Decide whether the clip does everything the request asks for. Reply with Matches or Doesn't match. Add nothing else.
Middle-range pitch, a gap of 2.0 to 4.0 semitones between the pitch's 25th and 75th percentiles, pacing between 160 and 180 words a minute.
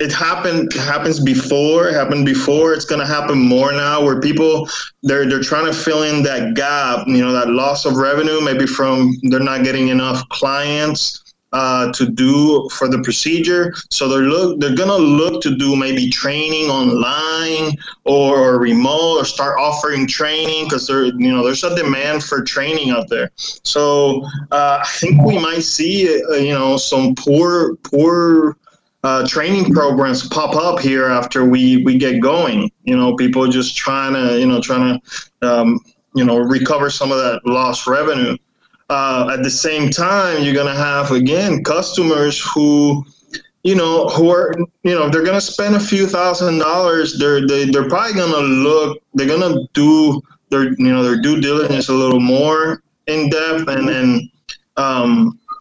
Matches